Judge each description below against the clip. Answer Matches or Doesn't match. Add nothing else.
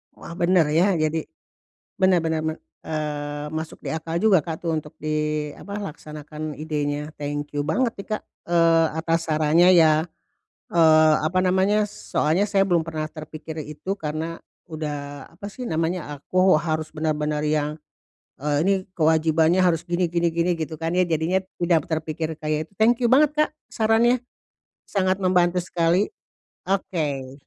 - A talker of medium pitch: Matches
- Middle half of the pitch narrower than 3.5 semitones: Matches